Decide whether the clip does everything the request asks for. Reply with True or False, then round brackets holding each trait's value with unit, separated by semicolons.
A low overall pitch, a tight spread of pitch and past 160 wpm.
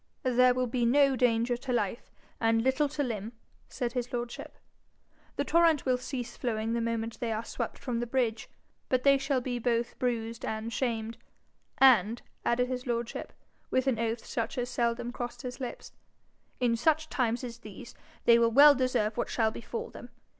False (240 Hz; 1.7 semitones; 180 wpm)